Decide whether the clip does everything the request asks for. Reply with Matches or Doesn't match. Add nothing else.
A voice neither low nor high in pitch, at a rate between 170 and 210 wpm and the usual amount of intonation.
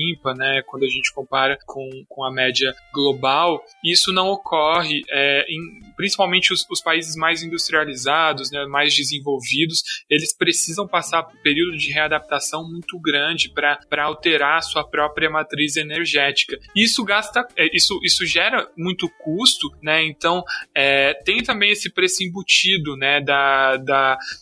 Doesn't match